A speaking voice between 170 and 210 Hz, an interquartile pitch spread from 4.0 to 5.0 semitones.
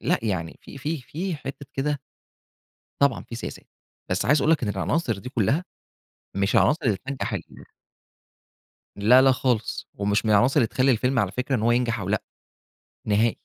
No: low, 125 Hz; average, 4.7 semitones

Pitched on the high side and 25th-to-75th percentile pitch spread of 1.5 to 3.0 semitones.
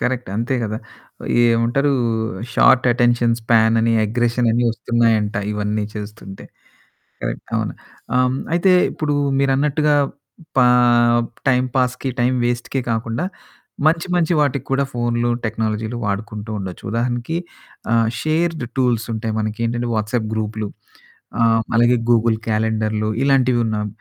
No: low, 120 Hz; narrow, 2.5 semitones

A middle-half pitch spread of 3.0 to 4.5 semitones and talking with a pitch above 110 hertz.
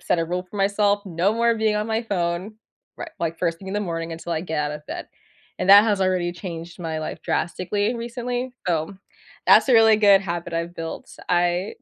Yes: average, 3.9 semitones; medium, 185 Hz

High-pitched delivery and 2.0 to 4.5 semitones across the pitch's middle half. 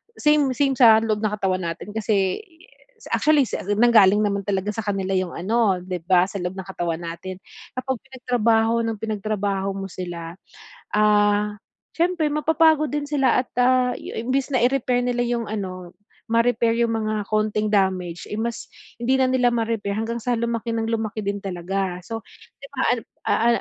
Yes: high, 220 Hz; average, 3.9 semitones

